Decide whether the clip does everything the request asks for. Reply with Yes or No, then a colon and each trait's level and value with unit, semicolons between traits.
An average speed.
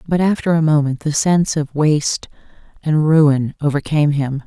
Yes: average, 160 wpm